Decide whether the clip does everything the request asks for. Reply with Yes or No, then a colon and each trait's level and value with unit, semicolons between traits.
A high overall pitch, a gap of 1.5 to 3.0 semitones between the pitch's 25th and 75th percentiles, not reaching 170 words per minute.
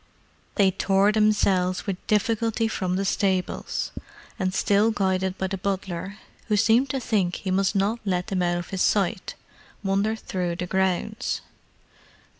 Yes: high, 195 Hz; narrow, 2.4 semitones; average, 150 wpm